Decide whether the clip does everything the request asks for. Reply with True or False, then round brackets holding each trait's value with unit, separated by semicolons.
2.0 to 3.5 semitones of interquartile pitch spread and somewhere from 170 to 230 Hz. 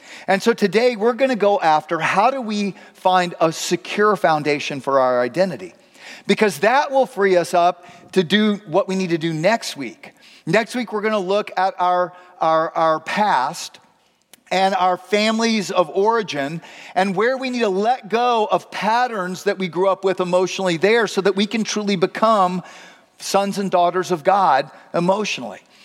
True (2.8 semitones; 190 Hz)